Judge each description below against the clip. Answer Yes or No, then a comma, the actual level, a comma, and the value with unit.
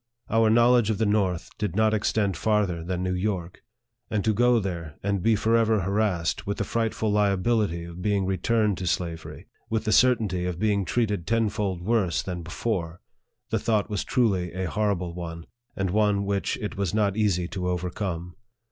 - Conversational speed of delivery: Yes, average, 175 wpm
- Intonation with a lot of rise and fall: No, average, 3.3 semitones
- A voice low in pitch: Yes, low, 100 Hz